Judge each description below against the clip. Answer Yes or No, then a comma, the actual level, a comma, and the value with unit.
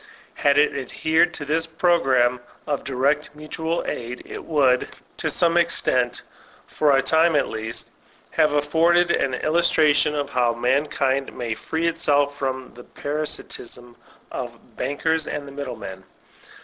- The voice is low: No, medium, 145 Hz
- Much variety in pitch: No, average, 3.8 semitones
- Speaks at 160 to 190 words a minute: No, average, 140 wpm